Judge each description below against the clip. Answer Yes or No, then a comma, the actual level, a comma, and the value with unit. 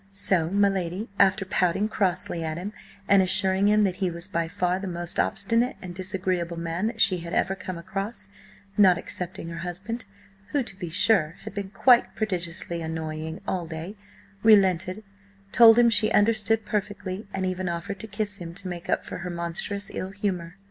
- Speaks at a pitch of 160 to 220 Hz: Yes, high, 190 Hz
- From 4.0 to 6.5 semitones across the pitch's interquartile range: No, average, 3.0 semitones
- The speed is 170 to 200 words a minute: Yes, average, 185 wpm